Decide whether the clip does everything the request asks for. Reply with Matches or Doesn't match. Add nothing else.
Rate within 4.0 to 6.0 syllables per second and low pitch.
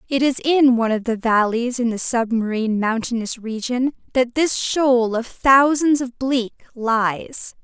Doesn't match